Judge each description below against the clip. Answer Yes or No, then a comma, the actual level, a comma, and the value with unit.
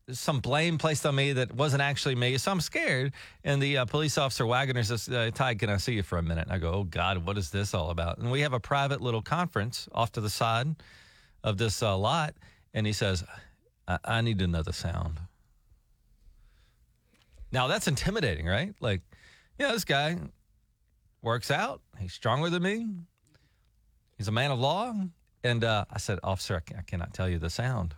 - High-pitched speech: No, low, 115 Hz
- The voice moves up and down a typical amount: No, wide, 6.0 semitones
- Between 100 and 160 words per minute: No, fast, 205 wpm